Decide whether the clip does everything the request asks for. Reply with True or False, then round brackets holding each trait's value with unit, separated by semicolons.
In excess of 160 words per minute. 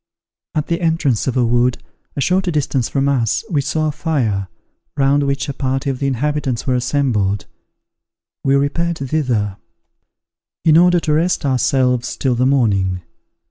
False (155 wpm)